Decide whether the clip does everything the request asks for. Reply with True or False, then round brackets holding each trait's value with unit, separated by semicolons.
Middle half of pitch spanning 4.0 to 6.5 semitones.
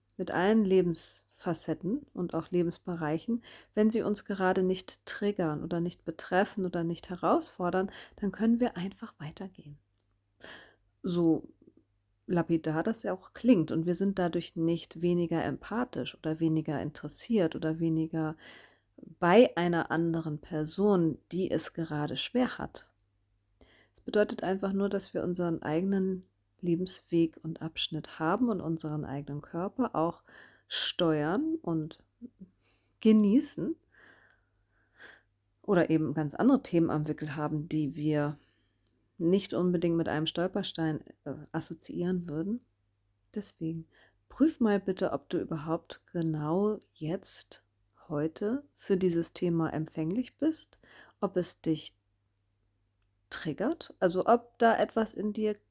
True (4.3 semitones)